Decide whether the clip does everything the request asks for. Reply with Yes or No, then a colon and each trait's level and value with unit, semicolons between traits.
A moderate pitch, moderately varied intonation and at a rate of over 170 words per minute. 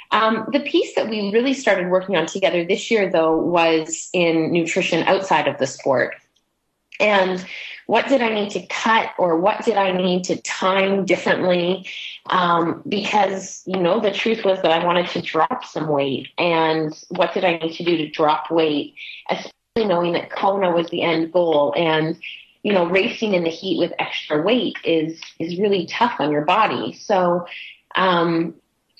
Yes: medium, 180 Hz; average, 3.2 semitones; average, 180 wpm